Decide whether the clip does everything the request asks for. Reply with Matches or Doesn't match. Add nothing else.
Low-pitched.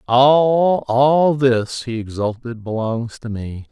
Matches